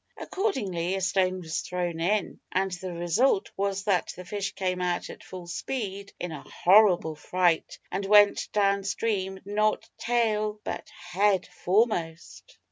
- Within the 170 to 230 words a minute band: No, average, 145 wpm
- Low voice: No, high, 190 Hz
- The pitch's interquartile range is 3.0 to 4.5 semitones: No, narrow, 2.6 semitones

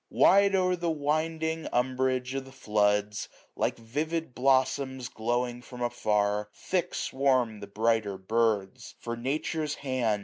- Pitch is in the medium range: No, low, 125 Hz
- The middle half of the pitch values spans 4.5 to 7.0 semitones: Yes, average, 4.9 semitones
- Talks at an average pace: No, slow, 130 wpm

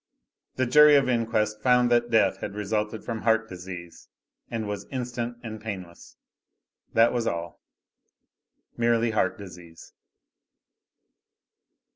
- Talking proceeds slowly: Yes, slow, 115 wpm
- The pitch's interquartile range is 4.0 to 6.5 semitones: No, average, 3.1 semitones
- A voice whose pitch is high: No, low, 110 Hz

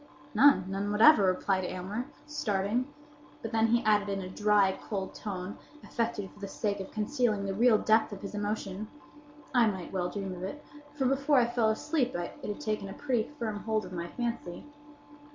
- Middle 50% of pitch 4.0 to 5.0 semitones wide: No, average, 3.4 semitones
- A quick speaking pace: No, average, 190 wpm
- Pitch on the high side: Yes, high, 210 Hz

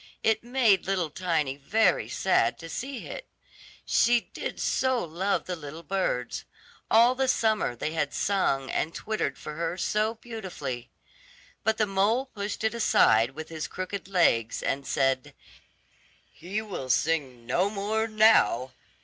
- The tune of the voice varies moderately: No, wide, 6.7 semitones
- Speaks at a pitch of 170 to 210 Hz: Yes, high, 190 Hz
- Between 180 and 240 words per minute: No, average, 145 wpm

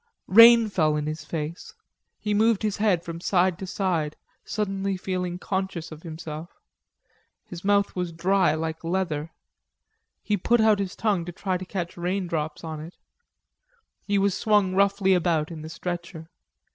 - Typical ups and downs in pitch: Yes, average, 3.3 semitones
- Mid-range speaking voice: Yes, medium, 180 Hz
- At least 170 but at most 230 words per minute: No, average, 160 wpm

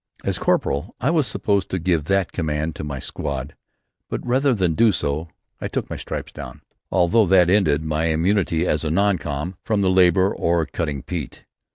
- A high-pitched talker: No, very low, 85 Hz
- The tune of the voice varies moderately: Yes, average, 4.1 semitones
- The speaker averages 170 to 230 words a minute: Yes, average, 190 wpm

